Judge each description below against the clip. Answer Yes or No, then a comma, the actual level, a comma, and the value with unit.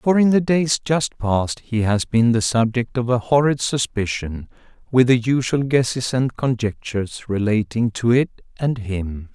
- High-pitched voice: No, low, 120 Hz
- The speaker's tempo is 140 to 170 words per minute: Yes, average, 165 wpm